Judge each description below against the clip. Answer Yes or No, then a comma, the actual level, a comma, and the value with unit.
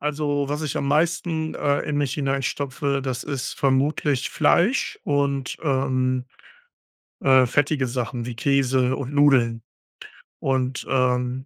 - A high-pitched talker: No, low, 135 Hz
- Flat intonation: Yes, narrow, 2.0 semitones